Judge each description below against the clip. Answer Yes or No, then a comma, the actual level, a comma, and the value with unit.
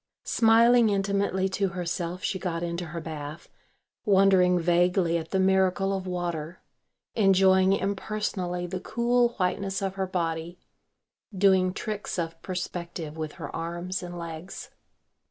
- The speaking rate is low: Yes, slow, 130 wpm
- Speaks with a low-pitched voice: No, medium, 185 Hz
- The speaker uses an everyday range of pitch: No, narrow, 2.2 semitones